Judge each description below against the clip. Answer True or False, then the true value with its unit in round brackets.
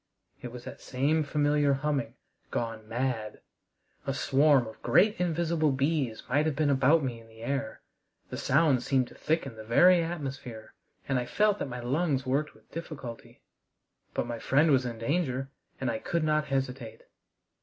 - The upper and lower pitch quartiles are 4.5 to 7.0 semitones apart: False (3.8 semitones)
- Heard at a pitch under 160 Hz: True (135 Hz)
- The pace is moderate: True (170 wpm)